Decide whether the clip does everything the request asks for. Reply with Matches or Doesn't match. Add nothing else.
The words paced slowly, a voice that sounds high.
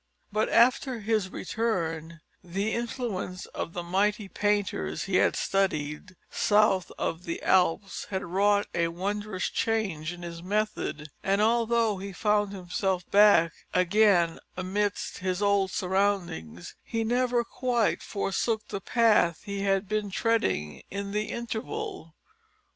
Matches